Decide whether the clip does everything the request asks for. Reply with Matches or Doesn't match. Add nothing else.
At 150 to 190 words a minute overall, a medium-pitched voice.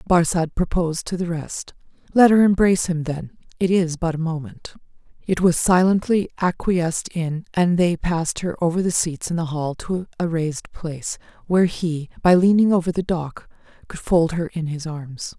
Matches